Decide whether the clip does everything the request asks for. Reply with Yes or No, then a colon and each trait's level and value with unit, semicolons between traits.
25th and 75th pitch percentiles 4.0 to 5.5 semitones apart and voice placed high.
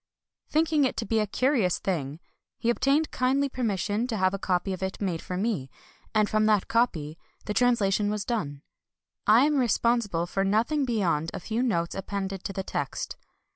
Yes: average, 4.3 semitones; high, 210 Hz